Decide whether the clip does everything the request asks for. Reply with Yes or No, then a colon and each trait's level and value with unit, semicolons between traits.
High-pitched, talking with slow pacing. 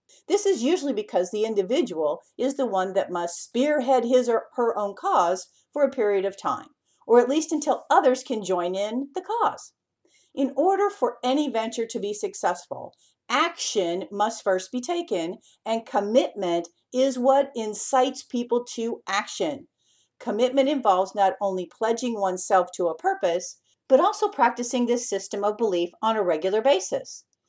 No: high, 235 Hz; average, 160 wpm